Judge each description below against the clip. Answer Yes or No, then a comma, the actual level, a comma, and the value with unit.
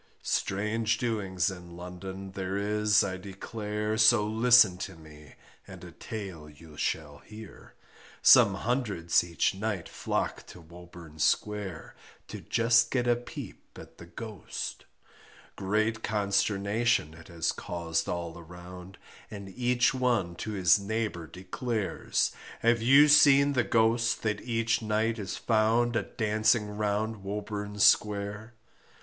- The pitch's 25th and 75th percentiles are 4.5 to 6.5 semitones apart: No, average, 3.7 semitones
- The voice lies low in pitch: Yes, low, 105 Hz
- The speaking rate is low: Yes, slow, 130 wpm